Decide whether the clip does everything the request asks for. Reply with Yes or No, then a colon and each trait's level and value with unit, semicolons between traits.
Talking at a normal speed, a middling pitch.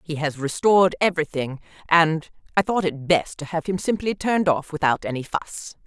Yes: average, 185 wpm; medium, 165 Hz